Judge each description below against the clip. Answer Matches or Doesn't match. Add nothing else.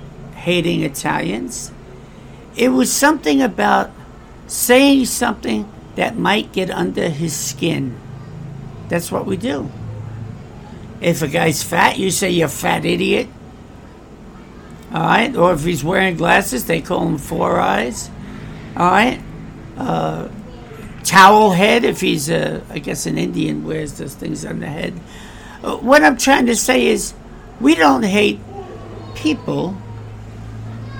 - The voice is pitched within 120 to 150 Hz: Doesn't match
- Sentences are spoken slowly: Matches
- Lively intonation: Matches